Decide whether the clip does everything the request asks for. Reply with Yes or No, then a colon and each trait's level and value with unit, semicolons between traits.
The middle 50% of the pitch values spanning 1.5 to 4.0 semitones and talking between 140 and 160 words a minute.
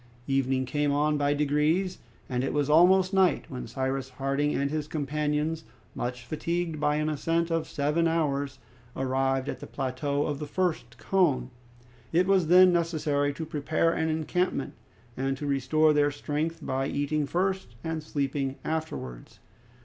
Yes: average, 3.0 semitones; average, 155 wpm